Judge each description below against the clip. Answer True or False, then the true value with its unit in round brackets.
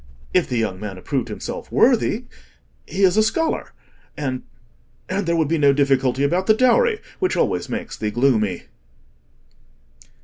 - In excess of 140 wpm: False (135 wpm)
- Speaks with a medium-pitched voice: True (145 Hz)